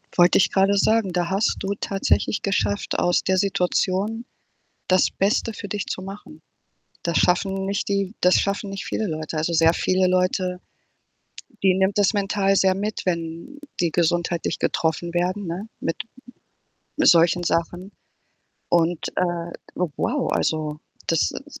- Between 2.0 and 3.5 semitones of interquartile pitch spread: Yes, narrow, 2.5 semitones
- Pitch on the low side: No, medium, 185 Hz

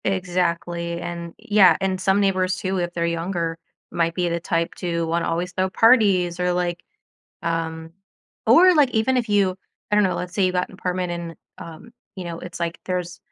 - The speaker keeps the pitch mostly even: Yes, narrow, 1.9 semitones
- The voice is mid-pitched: Yes, medium, 180 Hz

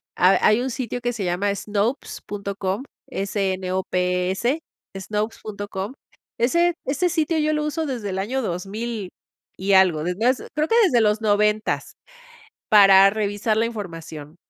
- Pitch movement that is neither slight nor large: Yes, average, 4.1 semitones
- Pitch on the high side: Yes, high, 210 Hz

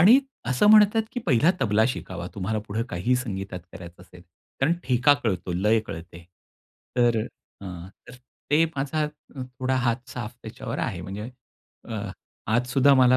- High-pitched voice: No, low, 120 Hz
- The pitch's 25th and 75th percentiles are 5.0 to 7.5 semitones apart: Yes, average, 5.3 semitones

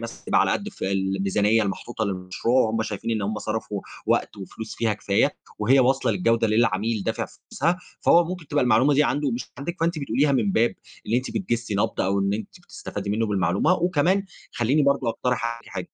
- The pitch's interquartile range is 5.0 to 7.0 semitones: Yes, average, 5.3 semitones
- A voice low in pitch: Yes, low, 115 Hz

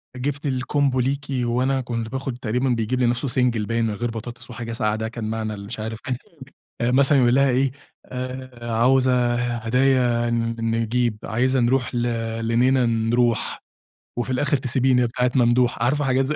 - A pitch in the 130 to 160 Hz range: No, low, 120 Hz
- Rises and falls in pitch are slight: Yes, narrow, 2.0 semitones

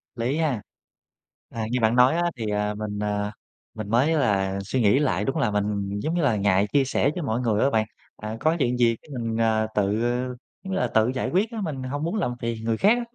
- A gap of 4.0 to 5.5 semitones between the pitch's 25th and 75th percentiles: Yes, average, 5.1 semitones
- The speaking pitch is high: No, low, 115 Hz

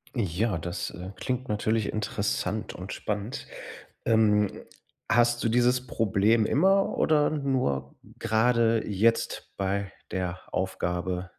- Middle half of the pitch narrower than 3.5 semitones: No, average, 4.0 semitones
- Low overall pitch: Yes, low, 110 Hz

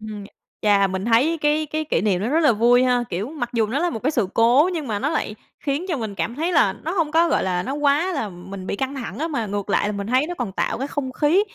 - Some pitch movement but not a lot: No, wide, 6.4 semitones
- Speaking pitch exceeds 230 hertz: Yes, very high, 250 Hz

